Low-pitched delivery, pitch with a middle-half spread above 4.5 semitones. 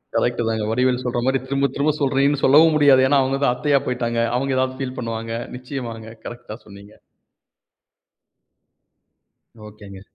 No: low, 125 Hz; average, 3.1 semitones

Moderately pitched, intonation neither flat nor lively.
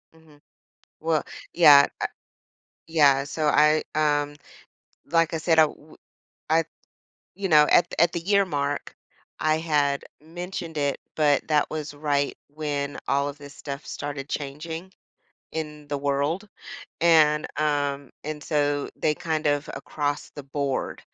No: medium, 150 Hz; narrow, 1.8 semitones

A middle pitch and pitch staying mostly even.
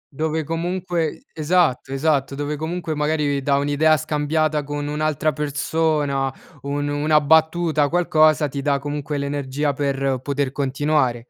Yes: medium, 145 Hz; narrow, 1.8 semitones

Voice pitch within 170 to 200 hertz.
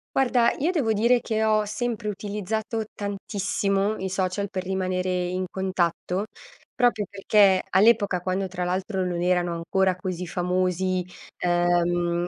Yes: high, 190 Hz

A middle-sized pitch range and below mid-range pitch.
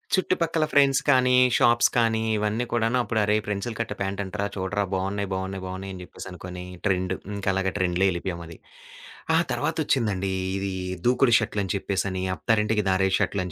Yes: average, 3.1 semitones; low, 100 Hz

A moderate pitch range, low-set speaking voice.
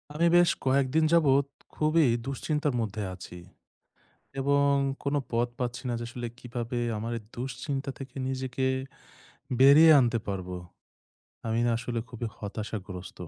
Yes: average, 3.4 semitones; low, 125 Hz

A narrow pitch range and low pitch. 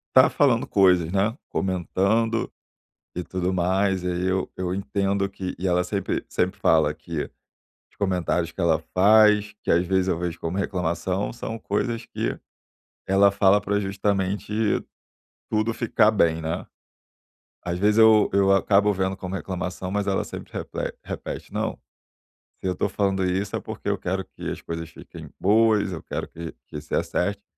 Yes: narrow, 2.2 semitones; very low, 95 Hz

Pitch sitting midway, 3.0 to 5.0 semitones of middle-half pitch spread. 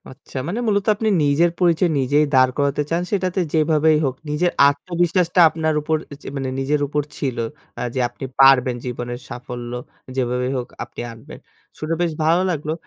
Yes: medium, 150 Hz; average, 4.6 semitones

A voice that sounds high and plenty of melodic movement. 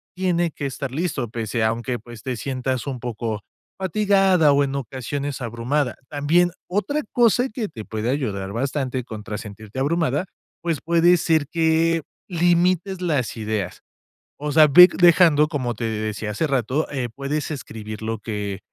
No: medium, 140 Hz; wide, 6.4 semitones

